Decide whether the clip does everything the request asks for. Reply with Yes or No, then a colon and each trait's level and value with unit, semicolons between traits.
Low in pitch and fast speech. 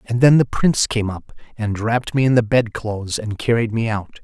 Yes: low, 115 Hz; fast, 225 wpm